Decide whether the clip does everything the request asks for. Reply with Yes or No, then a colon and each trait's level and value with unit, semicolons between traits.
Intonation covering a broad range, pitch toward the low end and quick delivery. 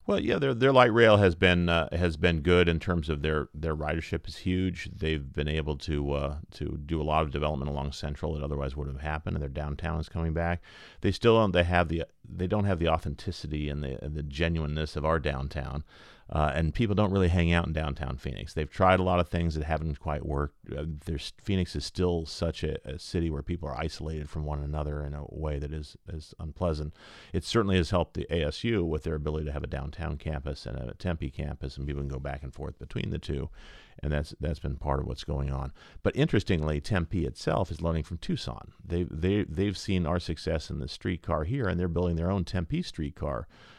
No: average, 3.2 semitones; very low, 80 Hz; fast, 230 wpm